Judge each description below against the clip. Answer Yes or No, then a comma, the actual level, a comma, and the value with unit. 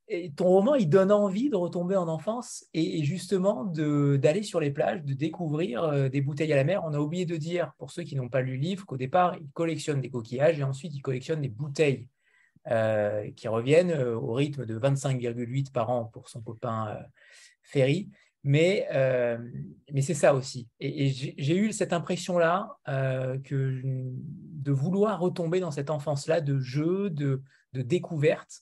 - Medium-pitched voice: Yes, medium, 150 Hz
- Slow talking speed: No, average, 185 wpm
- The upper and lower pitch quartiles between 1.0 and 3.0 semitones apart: No, average, 4.8 semitones